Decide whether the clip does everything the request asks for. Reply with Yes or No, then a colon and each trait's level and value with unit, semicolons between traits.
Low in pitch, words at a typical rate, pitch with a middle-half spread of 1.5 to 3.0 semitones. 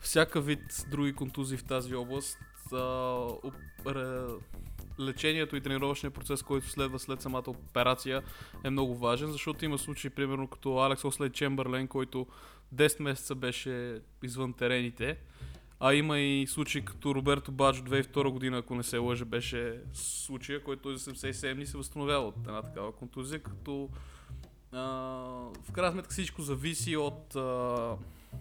Yes: low, 130 Hz; average, 145 wpm; narrow, 2.4 semitones